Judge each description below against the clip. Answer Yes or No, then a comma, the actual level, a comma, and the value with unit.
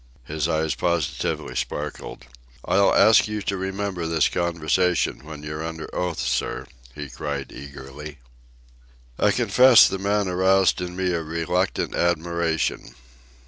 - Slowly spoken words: Yes, slow, 130 wpm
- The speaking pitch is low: Yes, very low, 85 Hz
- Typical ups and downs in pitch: Yes, average, 3.4 semitones